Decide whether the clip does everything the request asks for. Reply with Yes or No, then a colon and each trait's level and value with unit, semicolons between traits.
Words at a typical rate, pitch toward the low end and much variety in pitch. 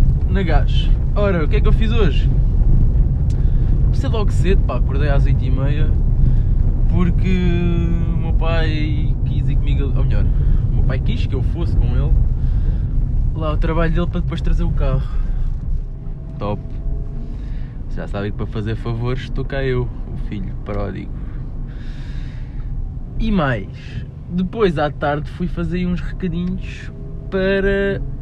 Yes: average, 140 wpm; low, 130 Hz; wide, 5.8 semitones